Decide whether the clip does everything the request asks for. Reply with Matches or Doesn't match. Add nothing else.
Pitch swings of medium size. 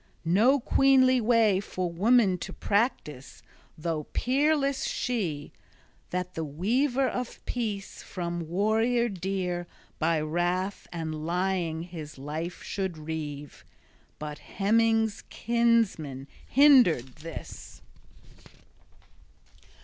Doesn't match